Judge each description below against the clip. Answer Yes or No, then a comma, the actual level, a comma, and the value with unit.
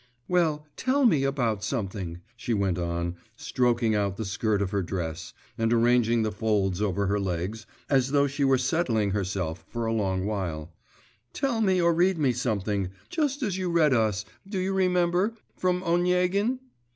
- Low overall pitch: Yes, low, 115 Hz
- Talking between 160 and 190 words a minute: Yes, average, 170 wpm